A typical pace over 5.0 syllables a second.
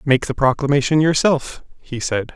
No: 4.7 syllables/s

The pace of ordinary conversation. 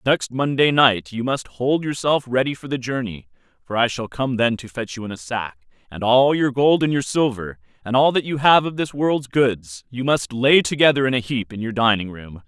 No: fast, 235 wpm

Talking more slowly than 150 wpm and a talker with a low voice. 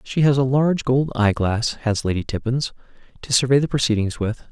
No: average, 200 wpm; low, 125 Hz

